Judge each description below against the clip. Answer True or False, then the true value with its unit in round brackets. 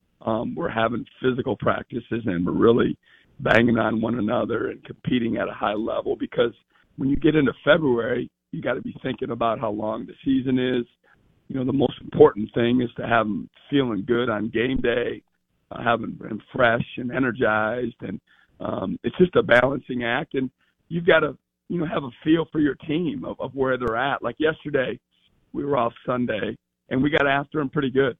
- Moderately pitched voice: False (125 Hz)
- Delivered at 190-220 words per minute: True (200 wpm)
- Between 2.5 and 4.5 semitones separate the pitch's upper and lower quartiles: True (3.8 semitones)